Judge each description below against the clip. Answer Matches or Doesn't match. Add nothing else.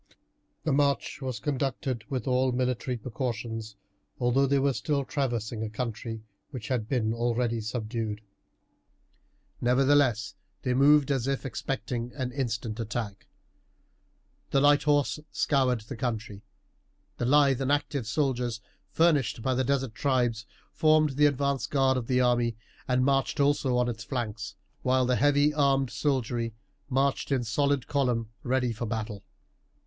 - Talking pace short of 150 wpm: Matches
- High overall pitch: Doesn't match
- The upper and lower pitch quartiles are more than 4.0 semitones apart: Doesn't match